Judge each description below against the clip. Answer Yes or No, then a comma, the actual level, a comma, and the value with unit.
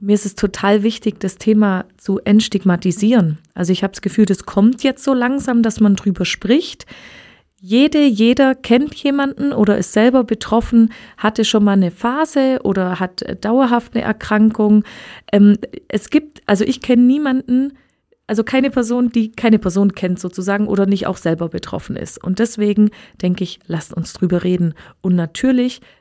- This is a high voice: Yes, high, 215 Hz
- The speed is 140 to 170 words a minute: Yes, average, 165 wpm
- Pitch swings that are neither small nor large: Yes, average, 4.0 semitones